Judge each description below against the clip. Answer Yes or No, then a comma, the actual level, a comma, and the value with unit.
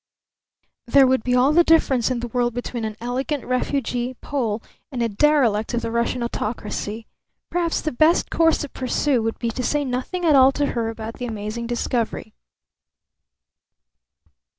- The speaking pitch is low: No, high, 245 Hz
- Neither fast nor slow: Yes, average, 165 wpm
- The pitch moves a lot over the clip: No, average, 3.3 semitones